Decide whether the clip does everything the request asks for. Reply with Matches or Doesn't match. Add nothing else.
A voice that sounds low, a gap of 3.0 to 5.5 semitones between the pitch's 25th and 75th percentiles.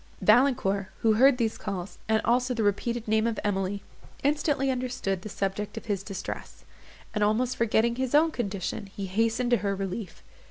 Doesn't match